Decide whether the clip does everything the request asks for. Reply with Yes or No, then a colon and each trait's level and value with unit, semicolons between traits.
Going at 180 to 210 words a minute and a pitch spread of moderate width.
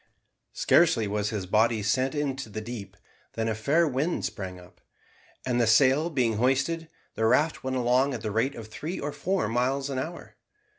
Yes: average, 185 wpm; average, 4.2 semitones